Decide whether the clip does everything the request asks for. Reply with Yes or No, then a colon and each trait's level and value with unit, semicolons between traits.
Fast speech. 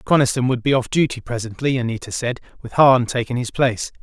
No: average, 195 wpm